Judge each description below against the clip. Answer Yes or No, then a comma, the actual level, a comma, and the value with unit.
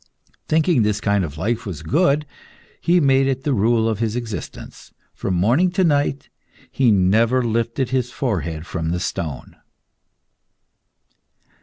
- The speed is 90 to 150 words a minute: Yes, average, 140 wpm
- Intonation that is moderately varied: No, wide, 5.8 semitones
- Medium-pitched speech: No, low, 115 Hz